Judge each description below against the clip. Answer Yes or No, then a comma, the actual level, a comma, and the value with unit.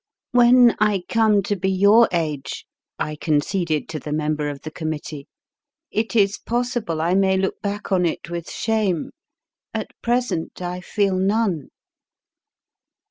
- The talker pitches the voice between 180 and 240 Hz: Yes, high, 190 Hz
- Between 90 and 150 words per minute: Yes, average, 140 wpm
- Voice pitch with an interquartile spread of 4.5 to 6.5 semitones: Yes, average, 5.0 semitones